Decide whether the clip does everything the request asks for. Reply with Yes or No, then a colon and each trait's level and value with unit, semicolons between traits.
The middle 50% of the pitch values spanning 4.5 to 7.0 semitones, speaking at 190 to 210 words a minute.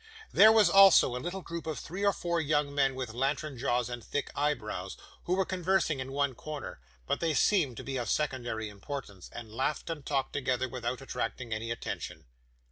Yes: average, 5.1 semitones; average, 195 wpm